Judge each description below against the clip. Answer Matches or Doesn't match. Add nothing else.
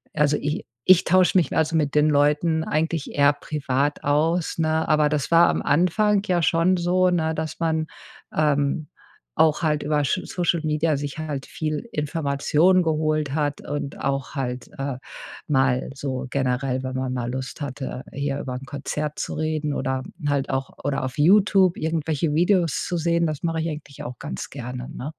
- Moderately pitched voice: Matches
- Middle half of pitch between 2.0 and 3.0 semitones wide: Matches